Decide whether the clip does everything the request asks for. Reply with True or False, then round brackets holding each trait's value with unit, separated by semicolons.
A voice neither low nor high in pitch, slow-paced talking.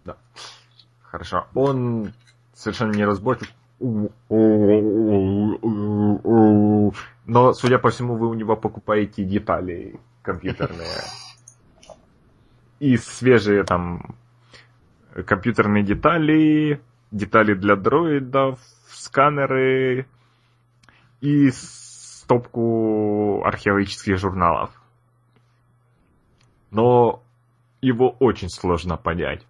False (120 Hz; 70 wpm)